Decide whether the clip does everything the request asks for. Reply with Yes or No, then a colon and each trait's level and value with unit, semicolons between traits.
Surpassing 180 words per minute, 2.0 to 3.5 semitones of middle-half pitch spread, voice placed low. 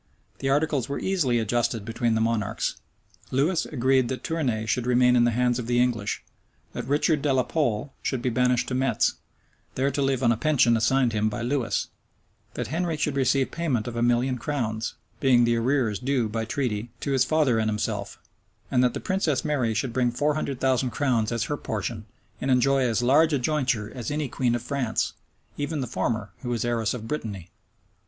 Yes: average, 200 wpm; average, 3.0 semitones; low, 125 Hz